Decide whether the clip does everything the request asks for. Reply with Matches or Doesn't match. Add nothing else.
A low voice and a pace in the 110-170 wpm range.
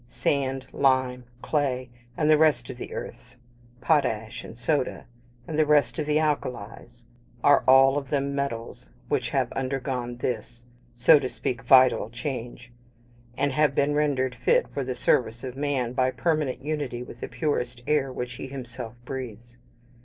Matches